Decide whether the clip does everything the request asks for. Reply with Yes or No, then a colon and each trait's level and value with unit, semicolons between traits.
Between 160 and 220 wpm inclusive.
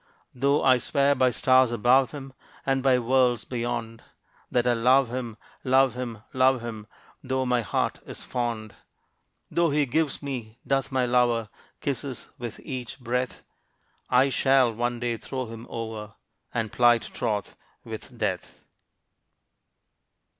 No: average, 140 wpm